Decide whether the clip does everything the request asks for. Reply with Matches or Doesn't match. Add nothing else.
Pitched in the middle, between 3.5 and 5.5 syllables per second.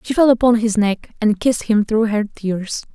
Doesn't match